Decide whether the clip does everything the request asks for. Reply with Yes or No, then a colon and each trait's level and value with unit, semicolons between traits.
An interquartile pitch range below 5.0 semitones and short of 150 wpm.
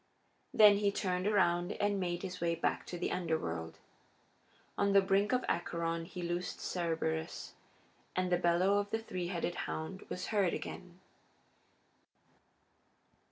Yes: narrow, 2.6 semitones; average, 140 wpm